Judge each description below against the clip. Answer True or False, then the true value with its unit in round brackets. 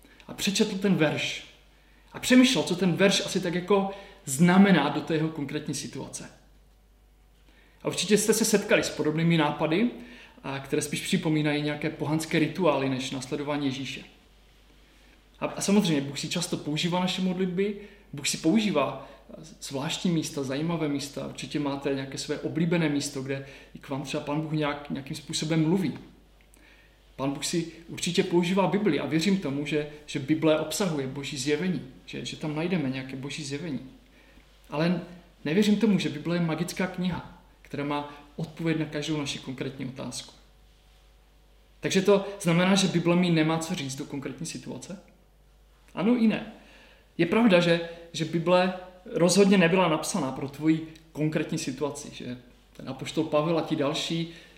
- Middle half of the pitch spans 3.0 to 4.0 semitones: True (3.7 semitones)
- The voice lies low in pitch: False (155 Hz)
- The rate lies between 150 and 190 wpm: True (155 wpm)